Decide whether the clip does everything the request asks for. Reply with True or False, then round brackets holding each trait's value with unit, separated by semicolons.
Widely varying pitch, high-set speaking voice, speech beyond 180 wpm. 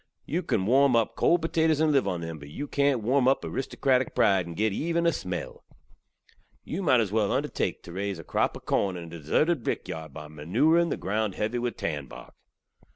False (8.2 semitones; 110 Hz; 205 wpm)